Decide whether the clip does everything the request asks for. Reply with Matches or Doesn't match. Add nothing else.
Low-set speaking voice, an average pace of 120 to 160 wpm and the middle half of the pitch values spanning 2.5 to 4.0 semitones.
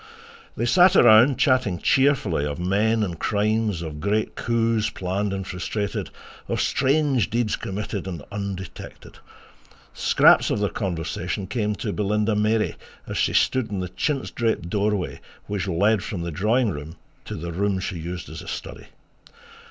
Matches